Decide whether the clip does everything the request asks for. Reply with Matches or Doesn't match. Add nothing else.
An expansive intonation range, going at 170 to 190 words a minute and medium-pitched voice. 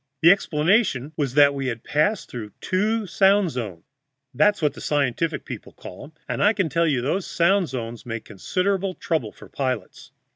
Matches